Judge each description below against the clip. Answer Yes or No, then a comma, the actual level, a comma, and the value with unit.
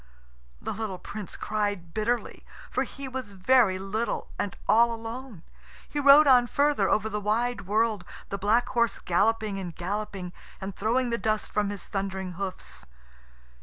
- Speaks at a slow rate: No, average, 155 wpm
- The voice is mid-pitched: No, high, 215 Hz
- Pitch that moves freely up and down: No, average, 3.4 semitones